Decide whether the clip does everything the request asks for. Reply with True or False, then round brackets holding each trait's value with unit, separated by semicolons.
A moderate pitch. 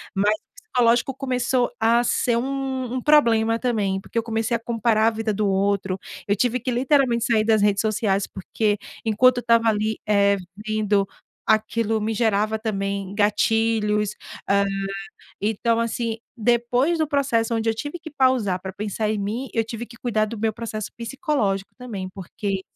False (225 Hz)